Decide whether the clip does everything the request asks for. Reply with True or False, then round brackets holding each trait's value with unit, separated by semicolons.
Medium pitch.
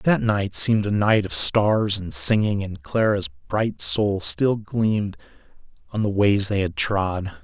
False (100 Hz)